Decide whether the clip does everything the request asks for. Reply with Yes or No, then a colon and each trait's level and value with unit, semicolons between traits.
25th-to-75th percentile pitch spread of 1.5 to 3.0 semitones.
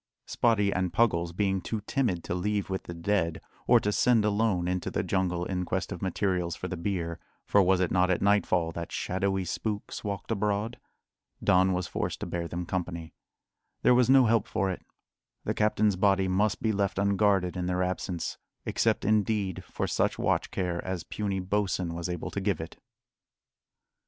Yes: narrow, 2.5 semitones